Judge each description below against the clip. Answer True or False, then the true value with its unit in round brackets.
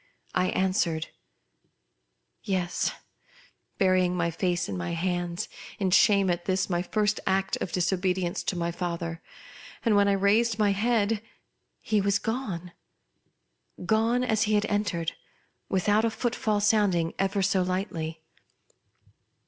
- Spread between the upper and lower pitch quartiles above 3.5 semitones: False (2.9 semitones)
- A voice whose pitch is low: False (190 Hz)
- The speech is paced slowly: True (130 wpm)